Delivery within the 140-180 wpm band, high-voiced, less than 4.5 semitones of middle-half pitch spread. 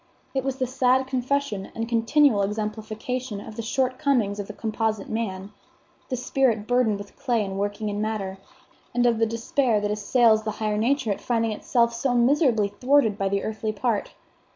Yes: average, 175 wpm; high, 225 Hz; average, 3.3 semitones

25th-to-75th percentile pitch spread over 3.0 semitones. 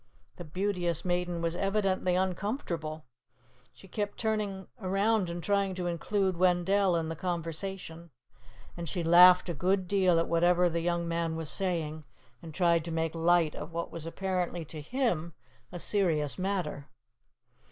No: narrow, 2.4 semitones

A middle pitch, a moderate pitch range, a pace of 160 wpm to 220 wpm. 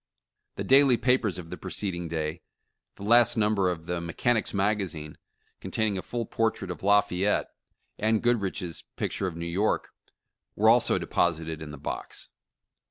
No: low, 100 Hz; average, 4.5 semitones; average, 165 wpm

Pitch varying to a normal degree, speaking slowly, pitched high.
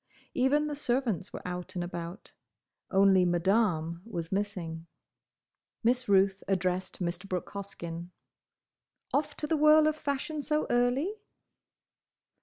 No: wide, 7.2 semitones; slow, 120 wpm; high, 195 Hz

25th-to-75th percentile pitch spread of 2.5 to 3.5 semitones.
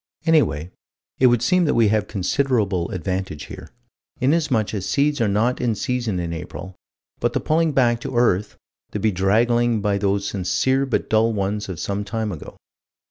No: average, 4.2 semitones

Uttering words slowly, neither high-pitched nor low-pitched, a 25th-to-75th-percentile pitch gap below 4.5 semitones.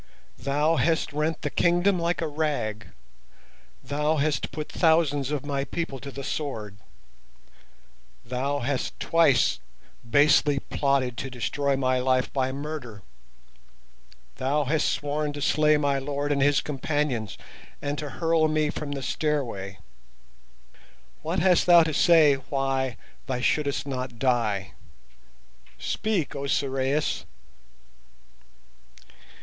Yes: slow, 120 wpm; medium, 145 Hz; narrow, 2.6 semitones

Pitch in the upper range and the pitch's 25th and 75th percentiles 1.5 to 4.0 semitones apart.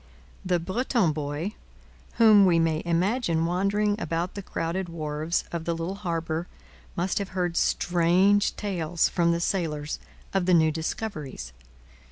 No: medium, 170 Hz; average, 2.9 semitones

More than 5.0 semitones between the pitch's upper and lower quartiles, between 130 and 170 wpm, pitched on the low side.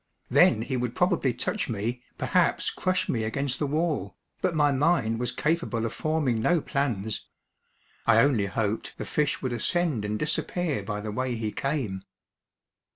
Yes: wide, 5.5 semitones; average, 160 wpm; low, 125 Hz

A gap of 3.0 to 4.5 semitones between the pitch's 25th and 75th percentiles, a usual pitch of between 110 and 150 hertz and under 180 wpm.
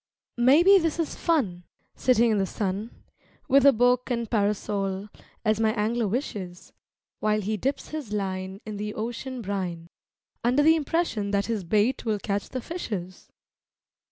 No: average, 4.2 semitones; high, 215 Hz; average, 155 wpm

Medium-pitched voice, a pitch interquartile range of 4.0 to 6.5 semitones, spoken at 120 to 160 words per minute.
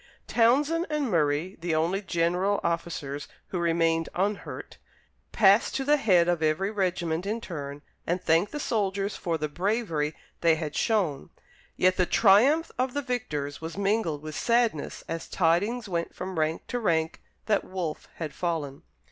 Yes: medium, 180 Hz; average, 4.7 semitones; average, 155 wpm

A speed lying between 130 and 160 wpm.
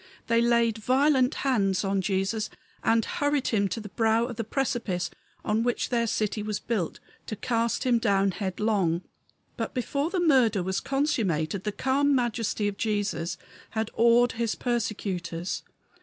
Yes: average, 155 wpm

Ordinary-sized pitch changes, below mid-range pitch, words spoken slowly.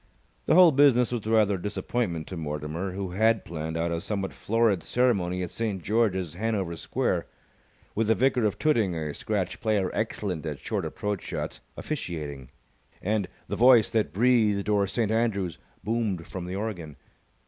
No: average, 4.3 semitones; low, 100 Hz; average, 165 wpm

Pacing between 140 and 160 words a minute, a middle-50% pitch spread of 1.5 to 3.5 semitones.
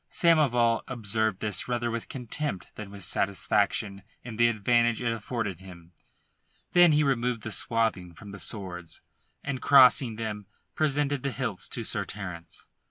No: average, 150 wpm; average, 4.0 semitones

